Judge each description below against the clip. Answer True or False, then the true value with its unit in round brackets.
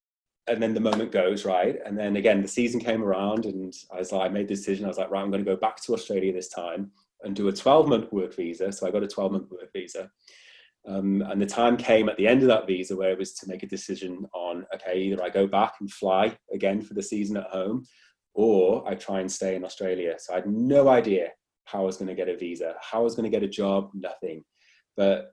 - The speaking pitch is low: True (100 Hz)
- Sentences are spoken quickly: True (265 wpm)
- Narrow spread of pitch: True (2.0 semitones)